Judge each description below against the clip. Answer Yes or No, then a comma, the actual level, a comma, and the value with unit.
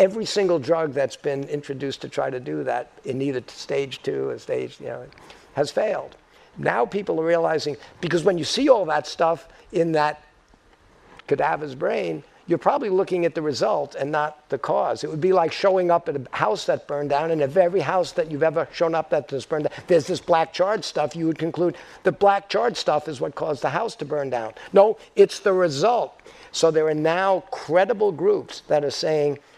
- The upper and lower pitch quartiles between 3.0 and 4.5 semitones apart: Yes, average, 4.2 semitones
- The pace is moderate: No, fast, 210 wpm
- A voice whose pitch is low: No, medium, 165 Hz